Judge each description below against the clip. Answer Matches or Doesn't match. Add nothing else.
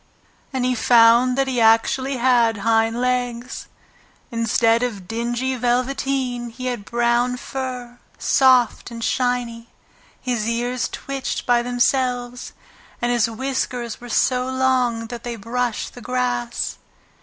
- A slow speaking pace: Matches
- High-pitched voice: Matches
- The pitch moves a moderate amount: Doesn't match